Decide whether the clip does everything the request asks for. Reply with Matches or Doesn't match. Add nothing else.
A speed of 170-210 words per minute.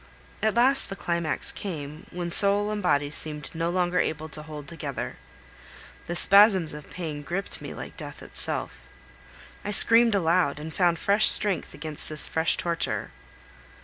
Doesn't match